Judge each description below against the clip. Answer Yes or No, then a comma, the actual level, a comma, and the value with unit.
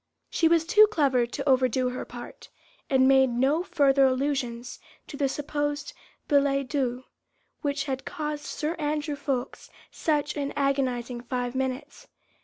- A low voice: No, very high, 275 Hz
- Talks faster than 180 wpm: No, average, 140 wpm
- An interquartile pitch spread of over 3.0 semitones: No, narrow, 2.5 semitones